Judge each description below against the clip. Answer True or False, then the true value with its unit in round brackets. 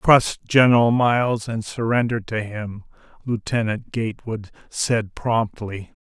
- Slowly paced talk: True (110 wpm)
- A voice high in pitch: False (115 Hz)